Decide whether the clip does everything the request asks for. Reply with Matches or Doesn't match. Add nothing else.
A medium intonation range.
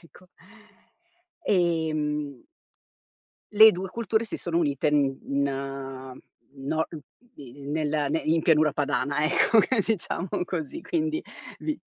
Matches